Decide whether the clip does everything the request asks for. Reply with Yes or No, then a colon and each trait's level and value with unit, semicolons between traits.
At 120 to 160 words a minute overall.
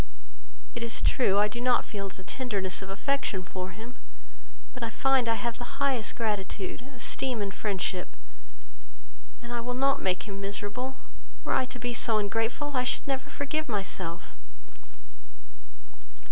Yes: average, 155 wpm